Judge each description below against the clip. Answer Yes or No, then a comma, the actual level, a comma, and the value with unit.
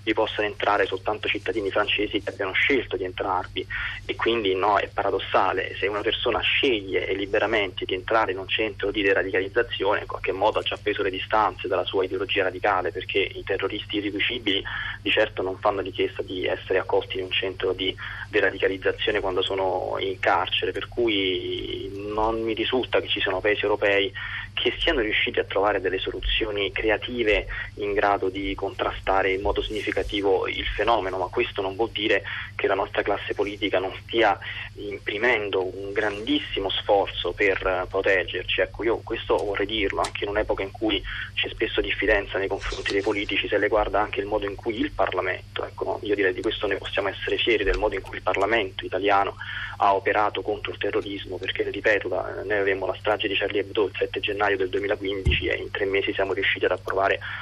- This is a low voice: No, very high, 365 Hz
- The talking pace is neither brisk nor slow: No, fast, 185 wpm